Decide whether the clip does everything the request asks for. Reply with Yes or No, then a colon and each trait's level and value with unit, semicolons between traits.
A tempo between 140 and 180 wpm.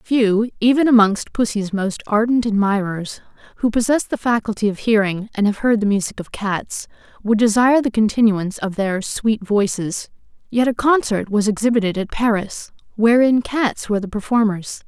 Yes: average, 160 wpm